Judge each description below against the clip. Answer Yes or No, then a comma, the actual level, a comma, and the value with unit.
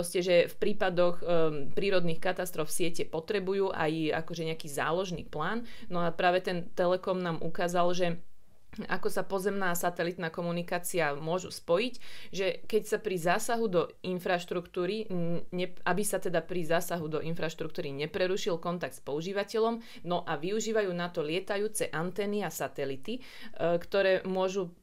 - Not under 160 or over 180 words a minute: No, average, 145 wpm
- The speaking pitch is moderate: Yes, medium, 180 Hz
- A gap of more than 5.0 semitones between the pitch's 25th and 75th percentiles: No, narrow, 2.6 semitones